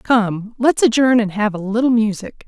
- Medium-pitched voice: No, high, 225 Hz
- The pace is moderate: Yes, average, 195 wpm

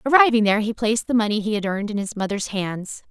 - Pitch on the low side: No, high, 215 Hz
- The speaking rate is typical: No, fast, 250 wpm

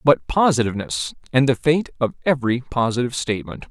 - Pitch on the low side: Yes, low, 125 Hz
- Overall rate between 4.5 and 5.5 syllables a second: No, 6.2 syllables/s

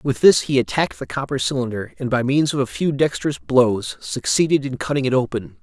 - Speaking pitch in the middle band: No, low, 130 Hz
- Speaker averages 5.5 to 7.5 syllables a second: Yes, 5.7 syllables/s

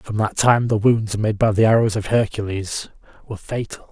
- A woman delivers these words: No, male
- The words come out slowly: No, average, 200 wpm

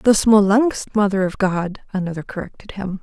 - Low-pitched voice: No, high, 200 Hz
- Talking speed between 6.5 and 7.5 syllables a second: No, 4.8 syllables/s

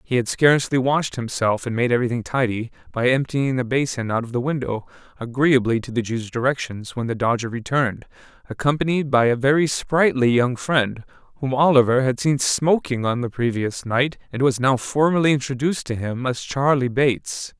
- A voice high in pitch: No, low, 130 Hz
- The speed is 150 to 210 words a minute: Yes, average, 180 wpm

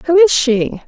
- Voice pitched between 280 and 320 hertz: Yes, very high, 285 Hz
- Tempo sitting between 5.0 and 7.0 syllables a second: No, 3.8 syllables/s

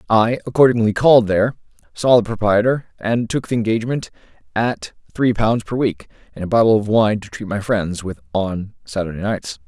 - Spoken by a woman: No, male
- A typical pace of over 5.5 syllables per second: No, 5.4 syllables/s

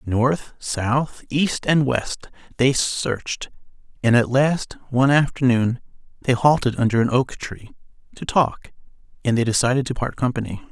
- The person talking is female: No, male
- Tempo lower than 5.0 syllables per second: Yes, 4.4 syllables/s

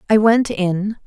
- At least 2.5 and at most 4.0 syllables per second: Yes, 3.7 syllables/s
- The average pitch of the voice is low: No, high, 205 Hz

